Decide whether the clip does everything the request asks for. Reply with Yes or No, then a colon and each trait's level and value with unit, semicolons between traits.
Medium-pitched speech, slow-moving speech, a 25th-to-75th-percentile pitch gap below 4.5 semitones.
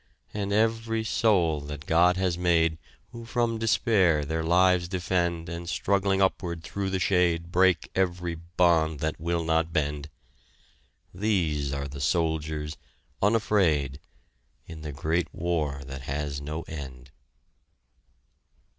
No: very low, 85 Hz; slow, 125 wpm; average, 3.5 semitones